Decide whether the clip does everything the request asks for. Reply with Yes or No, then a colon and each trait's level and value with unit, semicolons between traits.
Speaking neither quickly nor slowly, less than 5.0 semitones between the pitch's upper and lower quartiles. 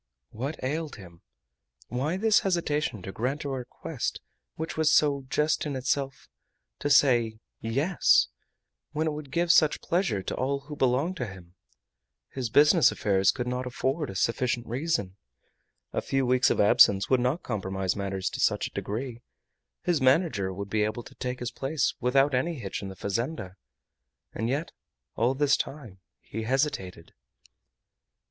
No: average, 160 wpm; wide, 5.4 semitones